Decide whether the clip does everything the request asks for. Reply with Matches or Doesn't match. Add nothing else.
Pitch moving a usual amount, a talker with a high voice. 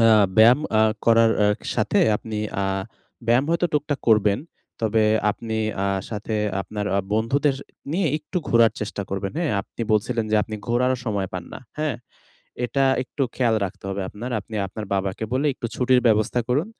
Doesn't match